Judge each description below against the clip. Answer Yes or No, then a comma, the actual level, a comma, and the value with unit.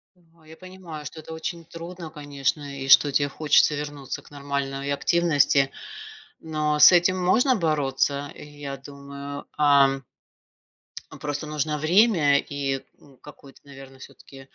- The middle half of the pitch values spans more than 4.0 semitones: No, narrow, 2.5 semitones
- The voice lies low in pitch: No, medium, 145 Hz